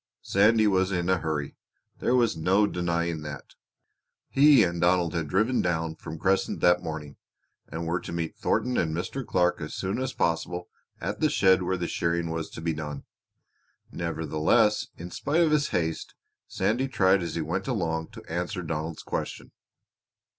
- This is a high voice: No, very low, 85 Hz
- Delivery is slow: No, average, 170 wpm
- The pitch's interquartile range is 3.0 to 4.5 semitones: Yes, average, 3.4 semitones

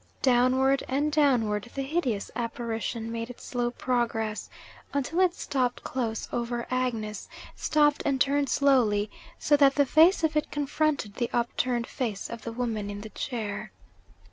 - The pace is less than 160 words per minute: Yes, average, 150 wpm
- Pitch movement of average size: Yes, average, 3.6 semitones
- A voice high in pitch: Yes, high, 245 Hz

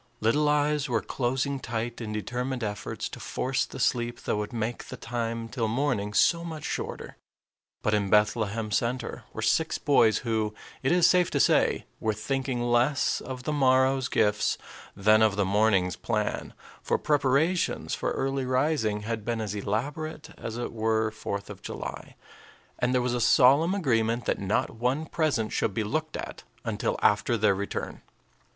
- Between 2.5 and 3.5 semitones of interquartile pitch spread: No, average, 4.0 semitones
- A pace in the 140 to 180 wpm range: Yes, average, 170 wpm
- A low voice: Yes, low, 120 Hz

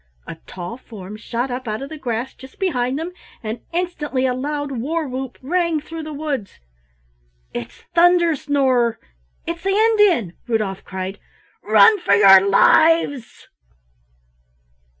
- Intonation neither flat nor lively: No, wide, 6.5 semitones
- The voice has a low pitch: No, very high, 265 Hz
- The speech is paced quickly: No, slow, 135 wpm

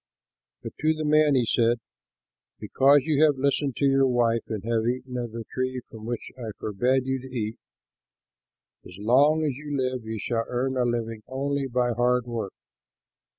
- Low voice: Yes, low, 125 Hz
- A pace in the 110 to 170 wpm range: No, average, 180 wpm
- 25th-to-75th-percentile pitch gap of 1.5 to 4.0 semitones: Yes, average, 2.8 semitones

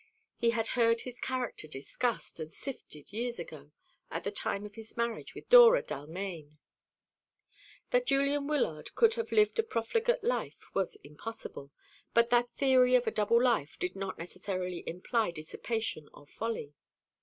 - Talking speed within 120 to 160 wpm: Yes, average, 155 wpm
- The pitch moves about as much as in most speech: No, wide, 6.2 semitones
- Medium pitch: No, high, 230 Hz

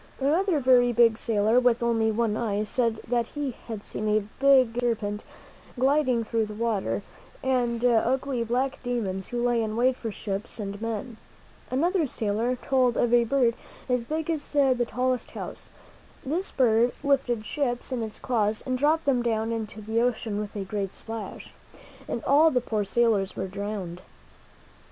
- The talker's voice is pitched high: Yes, high, 235 Hz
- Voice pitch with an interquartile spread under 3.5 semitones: Yes, average, 3.0 semitones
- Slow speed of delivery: No, average, 165 wpm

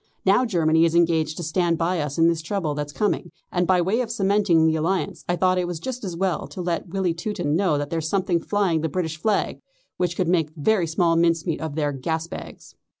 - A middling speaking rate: No, fast, 230 wpm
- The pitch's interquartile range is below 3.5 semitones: Yes, average, 2.7 semitones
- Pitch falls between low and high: Yes, medium, 170 Hz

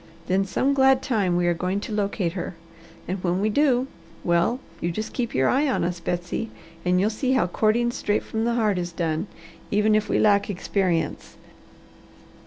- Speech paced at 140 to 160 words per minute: No, average, 190 wpm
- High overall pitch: Yes, high, 200 Hz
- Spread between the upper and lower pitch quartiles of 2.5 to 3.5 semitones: No, average, 4.4 semitones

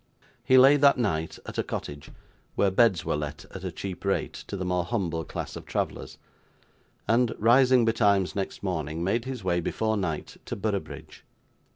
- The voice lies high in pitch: No, low, 100 Hz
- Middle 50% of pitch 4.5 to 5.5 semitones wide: Yes, average, 5.0 semitones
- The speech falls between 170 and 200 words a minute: Yes, average, 175 wpm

